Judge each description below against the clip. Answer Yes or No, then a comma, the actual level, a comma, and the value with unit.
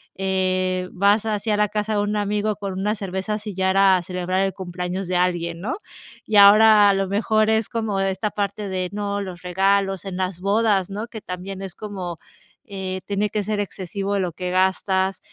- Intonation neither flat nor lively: No, narrow, 1.9 semitones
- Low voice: No, high, 195 Hz